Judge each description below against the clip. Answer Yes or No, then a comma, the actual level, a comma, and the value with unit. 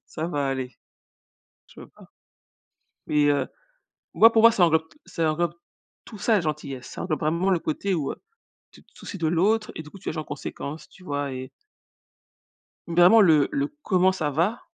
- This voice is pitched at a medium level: Yes, medium, 165 Hz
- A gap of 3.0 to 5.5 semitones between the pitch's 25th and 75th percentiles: Yes, average, 4.3 semitones